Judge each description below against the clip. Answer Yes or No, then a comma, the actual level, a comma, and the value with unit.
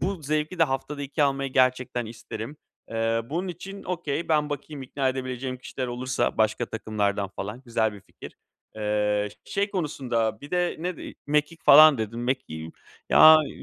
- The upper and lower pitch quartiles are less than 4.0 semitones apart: No, average, 5.2 semitones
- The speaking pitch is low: Yes, low, 130 Hz